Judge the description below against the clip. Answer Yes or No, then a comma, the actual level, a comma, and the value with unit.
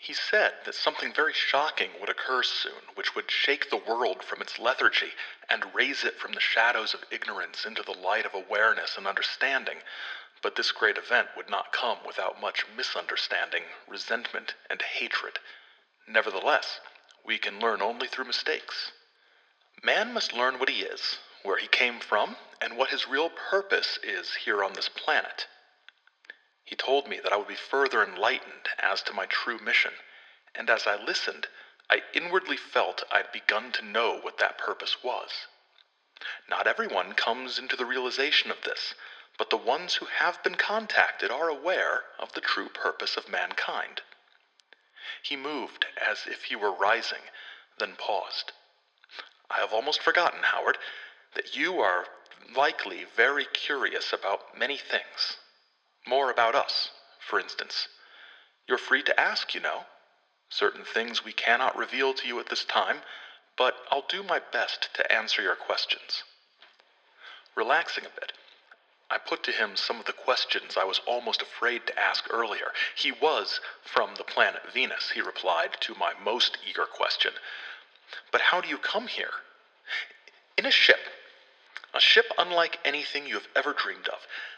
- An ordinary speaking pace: Yes, average, 160 wpm